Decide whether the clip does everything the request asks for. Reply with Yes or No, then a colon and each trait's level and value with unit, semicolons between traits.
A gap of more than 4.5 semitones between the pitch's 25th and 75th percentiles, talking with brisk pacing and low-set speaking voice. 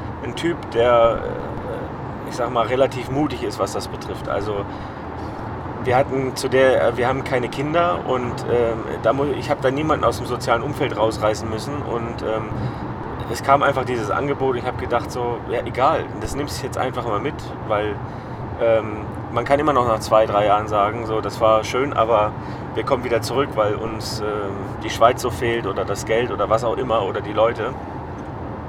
No: average, 3.0 semitones; fast, 195 wpm; low, 120 Hz